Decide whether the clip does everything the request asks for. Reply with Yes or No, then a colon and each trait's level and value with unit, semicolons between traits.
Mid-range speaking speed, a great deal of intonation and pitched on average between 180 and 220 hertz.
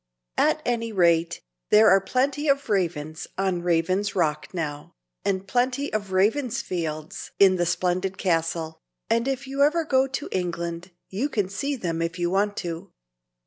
Yes: average, 155 wpm; wide, 6.3 semitones; high, 190 Hz